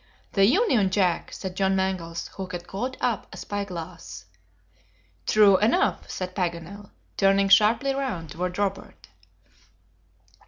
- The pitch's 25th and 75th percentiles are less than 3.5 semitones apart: Yes, narrow, 2.6 semitones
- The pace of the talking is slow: Yes, slow, 125 wpm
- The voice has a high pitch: Yes, high, 195 Hz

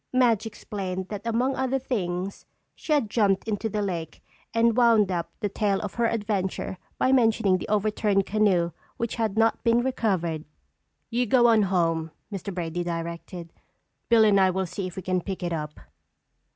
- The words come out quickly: No, average, 175 wpm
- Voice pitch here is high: Yes, high, 200 Hz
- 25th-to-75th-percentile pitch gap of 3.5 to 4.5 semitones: Yes, average, 3.9 semitones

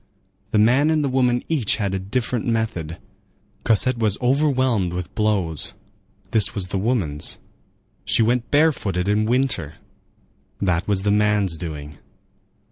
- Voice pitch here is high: No, low, 105 Hz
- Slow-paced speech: Yes, slow, 125 wpm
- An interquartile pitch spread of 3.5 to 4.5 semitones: No, average, 5.1 semitones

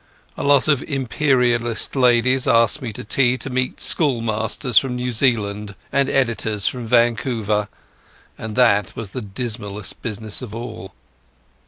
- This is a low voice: Yes, low, 120 Hz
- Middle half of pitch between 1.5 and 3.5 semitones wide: Yes, average, 3.0 semitones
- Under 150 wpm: Yes, average, 140 wpm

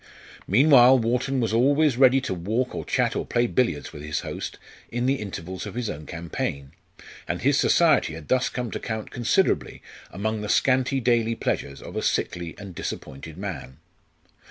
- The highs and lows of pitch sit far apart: Yes, wide, 6.4 semitones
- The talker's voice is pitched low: Yes, low, 115 Hz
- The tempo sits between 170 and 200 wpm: Yes, average, 175 wpm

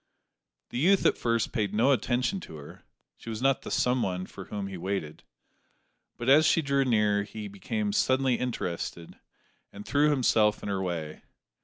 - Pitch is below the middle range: Yes, low, 110 Hz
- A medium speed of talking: Yes, average, 170 wpm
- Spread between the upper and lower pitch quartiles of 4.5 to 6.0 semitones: Yes, average, 4.9 semitones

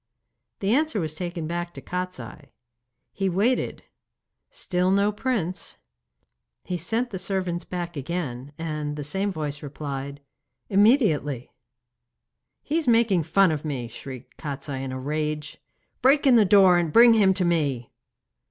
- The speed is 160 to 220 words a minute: No, average, 145 wpm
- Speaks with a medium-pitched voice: Yes, medium, 175 Hz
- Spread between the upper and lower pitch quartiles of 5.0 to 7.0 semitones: Yes, average, 5.3 semitones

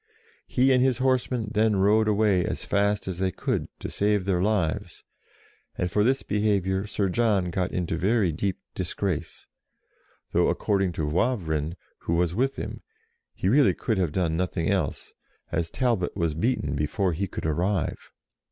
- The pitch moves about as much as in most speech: Yes, average, 3.8 semitones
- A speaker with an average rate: Yes, average, 160 wpm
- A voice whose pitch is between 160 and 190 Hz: No, very low, 95 Hz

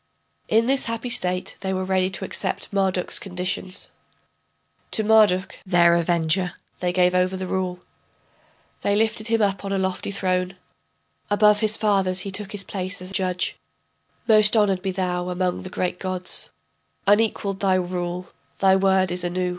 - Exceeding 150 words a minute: Yes, average, 160 wpm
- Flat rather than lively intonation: Yes, narrow, 1.8 semitones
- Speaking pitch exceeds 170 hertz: Yes, high, 190 Hz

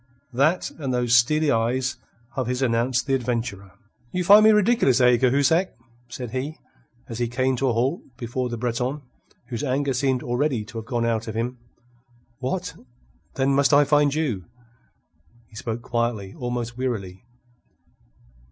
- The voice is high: No, low, 125 Hz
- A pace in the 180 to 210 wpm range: No, average, 155 wpm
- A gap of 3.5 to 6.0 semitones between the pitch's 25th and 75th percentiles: No, average, 2.8 semitones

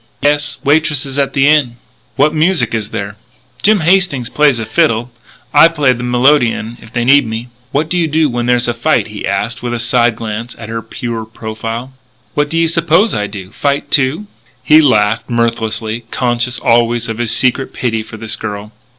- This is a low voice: Yes, low, 120 Hz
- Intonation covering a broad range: No, average, 4.5 semitones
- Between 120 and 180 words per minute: No, average, 190 wpm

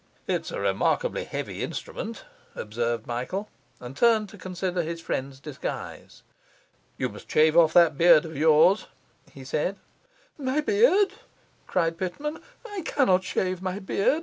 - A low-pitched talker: No, medium, 180 Hz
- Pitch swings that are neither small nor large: No, wide, 6.3 semitones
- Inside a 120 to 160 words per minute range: Yes, average, 140 wpm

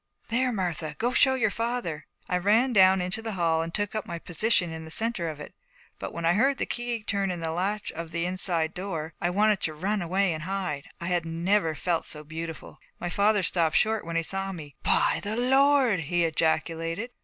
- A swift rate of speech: Yes, fast, 215 wpm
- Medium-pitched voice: Yes, medium, 180 Hz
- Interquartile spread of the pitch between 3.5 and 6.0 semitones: Yes, average, 4.4 semitones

